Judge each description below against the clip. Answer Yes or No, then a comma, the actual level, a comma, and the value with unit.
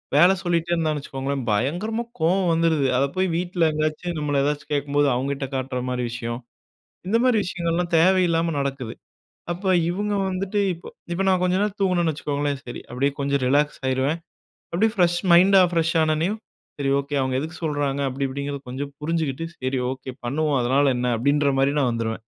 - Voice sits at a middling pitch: Yes, medium, 150 Hz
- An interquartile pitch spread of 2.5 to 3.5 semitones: No, average, 4.2 semitones